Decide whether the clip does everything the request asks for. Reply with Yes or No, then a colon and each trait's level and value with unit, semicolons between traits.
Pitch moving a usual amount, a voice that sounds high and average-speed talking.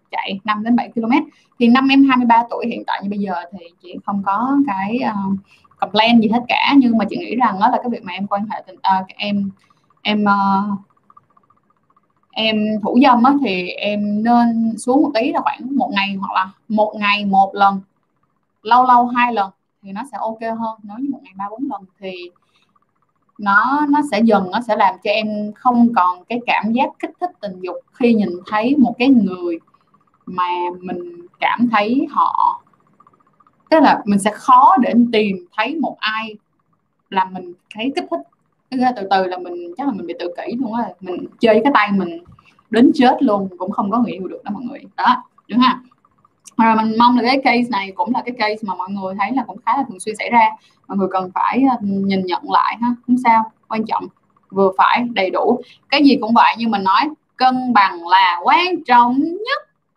Yes: average, 4.4 semitones; high, 220 Hz; average, 205 wpm